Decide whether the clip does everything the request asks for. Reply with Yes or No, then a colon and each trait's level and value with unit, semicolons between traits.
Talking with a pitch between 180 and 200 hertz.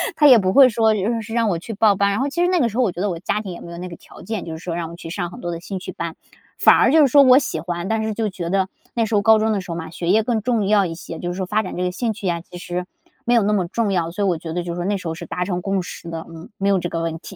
Yes: high, 190 Hz